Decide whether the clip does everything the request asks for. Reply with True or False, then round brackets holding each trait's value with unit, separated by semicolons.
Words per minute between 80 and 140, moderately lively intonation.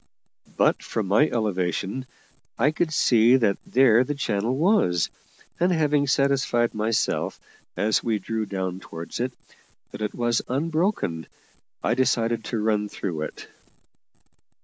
True (135 wpm; 4.8 semitones)